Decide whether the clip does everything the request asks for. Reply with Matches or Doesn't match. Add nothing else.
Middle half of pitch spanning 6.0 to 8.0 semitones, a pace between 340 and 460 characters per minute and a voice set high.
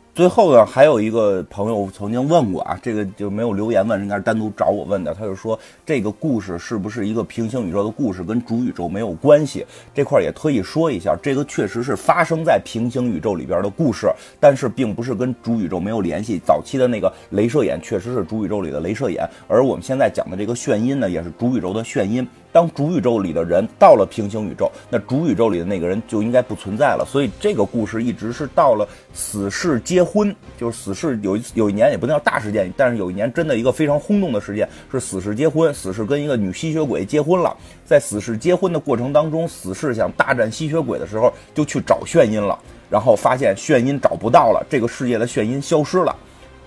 Doesn't match